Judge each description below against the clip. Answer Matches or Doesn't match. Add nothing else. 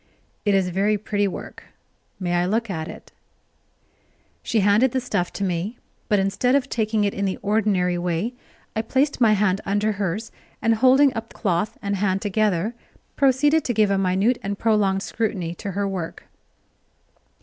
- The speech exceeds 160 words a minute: Matches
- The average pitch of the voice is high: Matches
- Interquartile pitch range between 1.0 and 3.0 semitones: Matches